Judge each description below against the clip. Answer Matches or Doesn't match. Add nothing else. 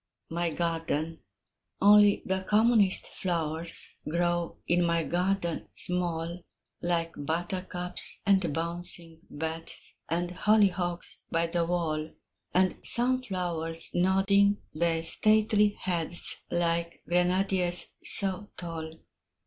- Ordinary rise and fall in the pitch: Doesn't match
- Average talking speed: Doesn't match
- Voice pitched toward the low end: Doesn't match